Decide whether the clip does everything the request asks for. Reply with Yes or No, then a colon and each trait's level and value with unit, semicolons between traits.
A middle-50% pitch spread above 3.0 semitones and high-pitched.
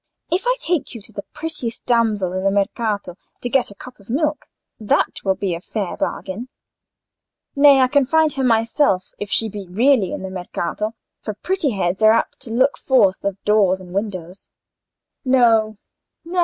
Yes: average, 5.1 semitones; high, 220 Hz